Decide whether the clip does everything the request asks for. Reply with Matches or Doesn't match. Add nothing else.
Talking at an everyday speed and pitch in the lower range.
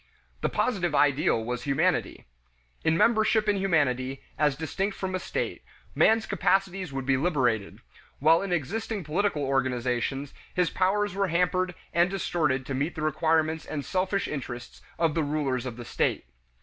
Doesn't match